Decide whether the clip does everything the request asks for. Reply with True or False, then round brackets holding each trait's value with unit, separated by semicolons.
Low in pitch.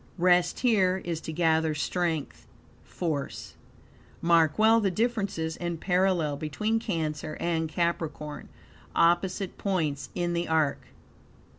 False (170 Hz)